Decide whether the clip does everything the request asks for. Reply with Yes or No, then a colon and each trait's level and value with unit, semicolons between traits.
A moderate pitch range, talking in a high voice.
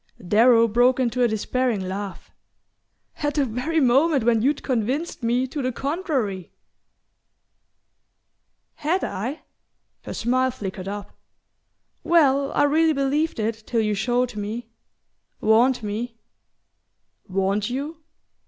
Yes: average, 4.3 semitones; high, 245 Hz